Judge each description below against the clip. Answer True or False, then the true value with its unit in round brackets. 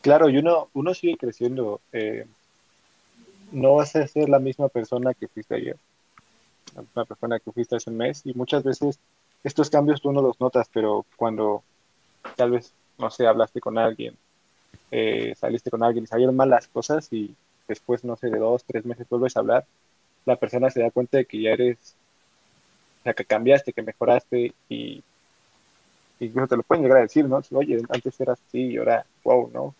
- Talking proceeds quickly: True (195 wpm)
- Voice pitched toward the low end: True (125 Hz)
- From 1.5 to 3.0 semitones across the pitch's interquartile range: True (2.7 semitones)